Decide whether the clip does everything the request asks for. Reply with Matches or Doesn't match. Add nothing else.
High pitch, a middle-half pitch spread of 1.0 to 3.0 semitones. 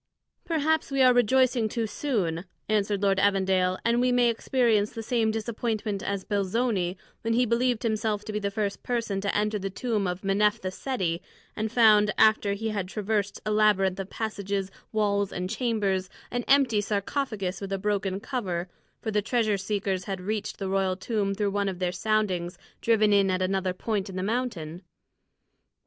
Matches